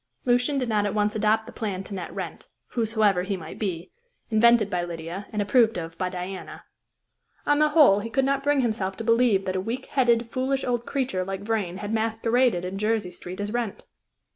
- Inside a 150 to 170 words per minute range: No, fast, 205 wpm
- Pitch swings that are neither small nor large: Yes, average, 4.0 semitones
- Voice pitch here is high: Yes, high, 215 Hz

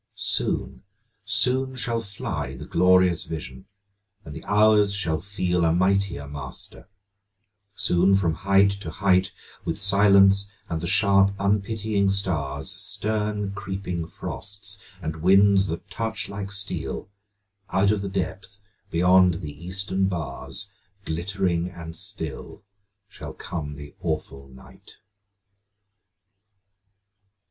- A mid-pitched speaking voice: No, very low, 95 Hz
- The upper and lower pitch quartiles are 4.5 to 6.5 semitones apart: No, average, 3.3 semitones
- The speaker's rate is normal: No, slow, 115 wpm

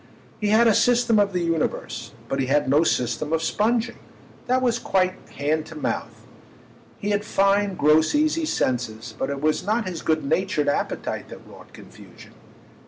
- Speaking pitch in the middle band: Yes, medium, 180 Hz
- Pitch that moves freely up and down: Yes, wide, 6.3 semitones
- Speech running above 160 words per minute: Yes, average, 170 wpm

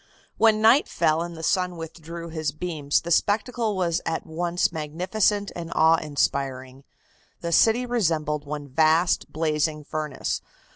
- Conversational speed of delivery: Yes, average, 145 wpm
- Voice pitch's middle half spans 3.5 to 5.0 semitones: No, average, 3.0 semitones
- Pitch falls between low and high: Yes, medium, 165 Hz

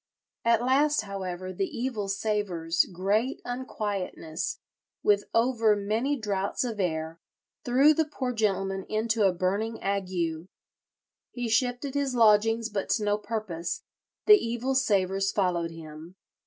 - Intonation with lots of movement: No, average, 4.1 semitones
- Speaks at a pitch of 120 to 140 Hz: No, high, 210 Hz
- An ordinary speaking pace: No, slow, 130 wpm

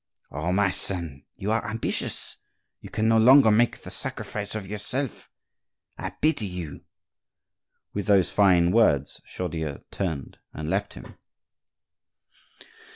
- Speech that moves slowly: Yes, slow, 120 wpm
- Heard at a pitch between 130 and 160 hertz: No, low, 100 Hz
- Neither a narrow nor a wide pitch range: Yes, average, 4.6 semitones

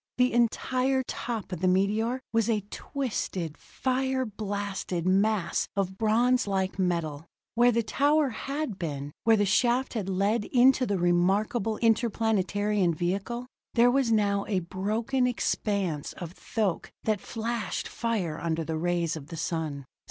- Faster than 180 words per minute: No, average, 145 wpm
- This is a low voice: No, high, 210 Hz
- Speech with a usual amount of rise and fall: Yes, average, 4.7 semitones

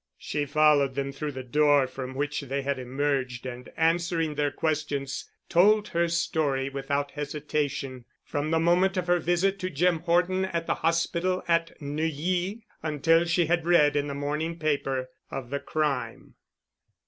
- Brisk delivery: No, average, 160 wpm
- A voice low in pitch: No, medium, 150 Hz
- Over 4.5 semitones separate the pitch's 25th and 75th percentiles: No, average, 3.3 semitones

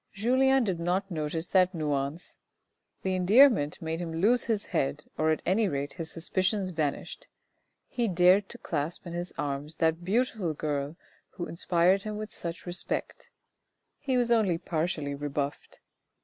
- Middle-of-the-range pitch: Yes, medium, 175 Hz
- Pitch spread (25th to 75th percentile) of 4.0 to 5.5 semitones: Yes, average, 4.4 semitones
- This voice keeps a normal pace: Yes, average, 150 wpm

